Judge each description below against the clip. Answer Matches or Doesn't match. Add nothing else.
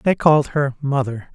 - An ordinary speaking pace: Matches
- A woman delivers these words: Doesn't match